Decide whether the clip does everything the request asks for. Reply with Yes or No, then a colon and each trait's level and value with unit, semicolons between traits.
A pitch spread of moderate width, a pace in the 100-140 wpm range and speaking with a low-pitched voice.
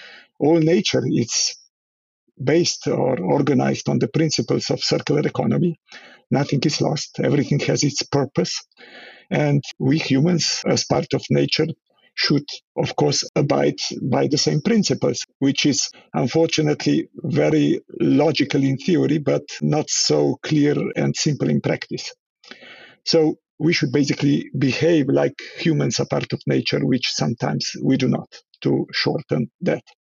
No: average, 3.6 semitones; slow, 135 wpm; medium, 150 Hz